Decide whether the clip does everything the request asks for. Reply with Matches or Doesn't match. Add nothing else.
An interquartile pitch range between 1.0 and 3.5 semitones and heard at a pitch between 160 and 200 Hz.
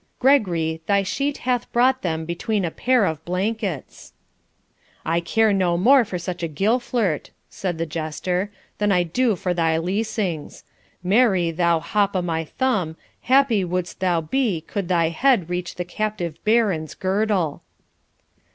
Doesn't match